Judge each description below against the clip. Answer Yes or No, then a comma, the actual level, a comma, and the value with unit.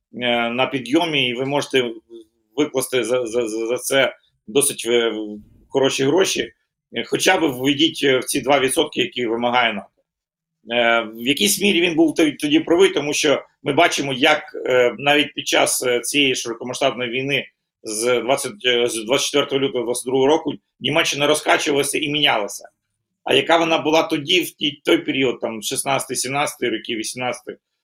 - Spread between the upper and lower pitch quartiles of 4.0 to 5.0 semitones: No, average, 3.6 semitones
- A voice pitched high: No, low, 135 Hz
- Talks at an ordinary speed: Yes, average, 135 wpm